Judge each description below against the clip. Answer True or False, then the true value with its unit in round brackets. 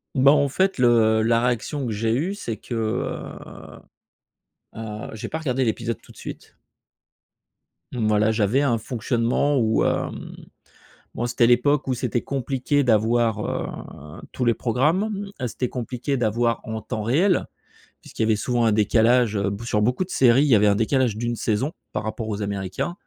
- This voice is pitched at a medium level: False (120 Hz)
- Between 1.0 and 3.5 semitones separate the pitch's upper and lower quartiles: True (3.2 semitones)